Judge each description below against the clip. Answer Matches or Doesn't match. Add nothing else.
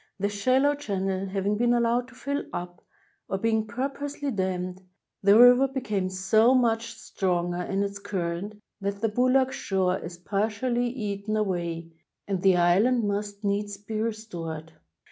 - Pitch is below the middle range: Doesn't match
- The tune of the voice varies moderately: Matches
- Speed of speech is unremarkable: Matches